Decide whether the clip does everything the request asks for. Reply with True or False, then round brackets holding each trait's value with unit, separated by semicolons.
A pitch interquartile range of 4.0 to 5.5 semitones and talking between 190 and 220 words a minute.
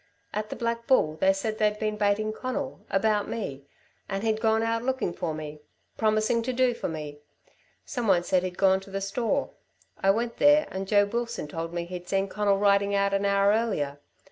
False (3.1 semitones; 200 wpm)